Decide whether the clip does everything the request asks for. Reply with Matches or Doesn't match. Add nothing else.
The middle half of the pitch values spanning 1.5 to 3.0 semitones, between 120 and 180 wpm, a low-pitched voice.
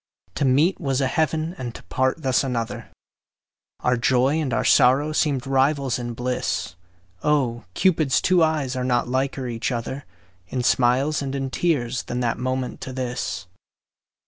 Matches